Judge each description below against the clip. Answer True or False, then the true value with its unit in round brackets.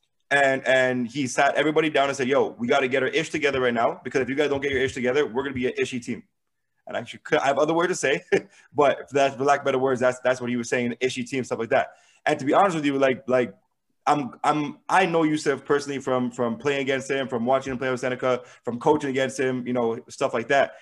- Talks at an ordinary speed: False (270 wpm)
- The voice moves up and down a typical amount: False (2.0 semitones)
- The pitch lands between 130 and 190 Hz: True (135 Hz)